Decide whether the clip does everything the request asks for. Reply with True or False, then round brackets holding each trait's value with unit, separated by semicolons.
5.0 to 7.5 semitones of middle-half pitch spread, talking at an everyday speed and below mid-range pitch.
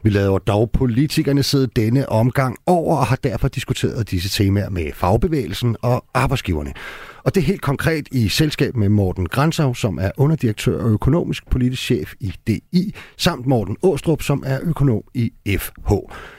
True (5.3 semitones; 165 wpm; 125 Hz)